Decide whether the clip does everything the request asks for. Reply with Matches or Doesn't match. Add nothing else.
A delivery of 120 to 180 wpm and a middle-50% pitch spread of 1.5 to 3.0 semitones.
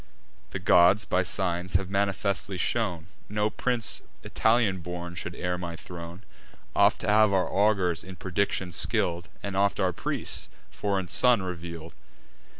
Matches